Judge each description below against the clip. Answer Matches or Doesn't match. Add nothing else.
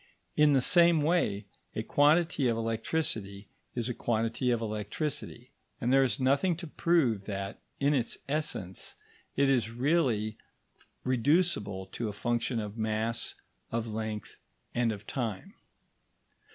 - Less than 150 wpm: Matches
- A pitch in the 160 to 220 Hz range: Doesn't match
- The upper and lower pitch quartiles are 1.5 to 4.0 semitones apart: Doesn't match